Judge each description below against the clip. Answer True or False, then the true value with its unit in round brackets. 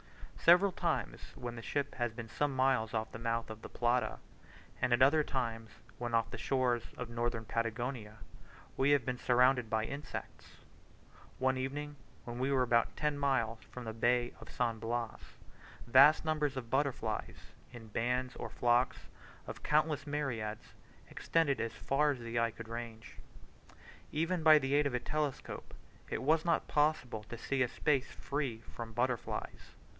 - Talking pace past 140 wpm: True (165 wpm)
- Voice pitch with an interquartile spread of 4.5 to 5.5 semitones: False (3.4 semitones)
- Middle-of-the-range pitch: False (125 Hz)